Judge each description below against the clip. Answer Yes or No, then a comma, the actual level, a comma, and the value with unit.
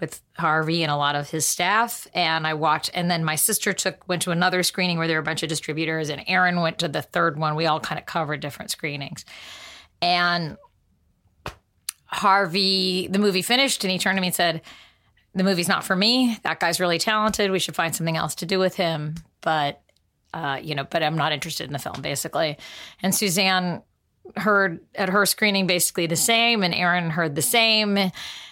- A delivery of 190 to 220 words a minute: Yes, fast, 205 wpm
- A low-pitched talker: No, medium, 175 Hz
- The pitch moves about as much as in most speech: Yes, average, 3.3 semitones